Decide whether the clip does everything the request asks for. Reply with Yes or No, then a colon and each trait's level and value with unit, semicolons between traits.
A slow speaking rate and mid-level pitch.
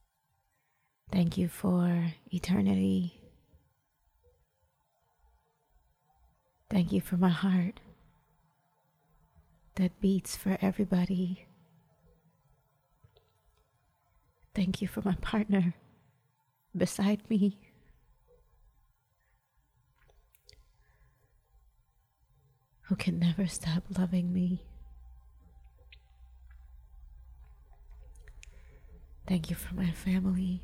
Yes: slow, 60 wpm; medium, 170 Hz